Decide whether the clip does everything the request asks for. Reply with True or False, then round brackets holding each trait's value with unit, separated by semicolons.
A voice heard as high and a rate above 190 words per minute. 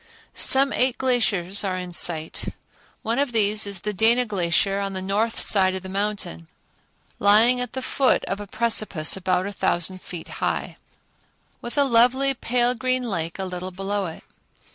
False (205 Hz; 170 wpm)